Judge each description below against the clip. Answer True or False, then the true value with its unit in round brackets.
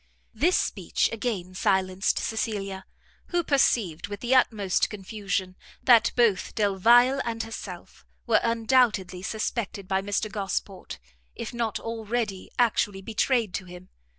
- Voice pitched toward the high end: True (215 Hz)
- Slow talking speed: True (125 wpm)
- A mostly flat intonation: False (3.4 semitones)